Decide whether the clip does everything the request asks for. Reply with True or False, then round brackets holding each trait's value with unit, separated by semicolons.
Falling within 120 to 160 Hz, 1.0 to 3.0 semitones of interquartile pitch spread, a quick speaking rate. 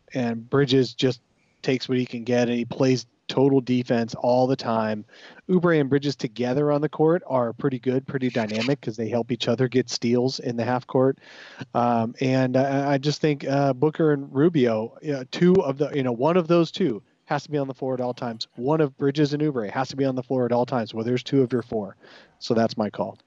True (130 Hz; 2.7 semitones; 235 wpm)